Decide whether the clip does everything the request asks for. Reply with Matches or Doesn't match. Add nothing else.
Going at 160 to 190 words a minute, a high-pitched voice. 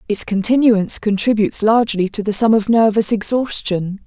Doesn't match